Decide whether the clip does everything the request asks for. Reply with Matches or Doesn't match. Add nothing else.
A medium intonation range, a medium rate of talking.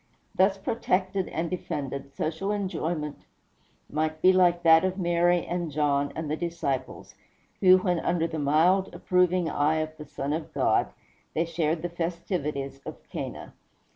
Matches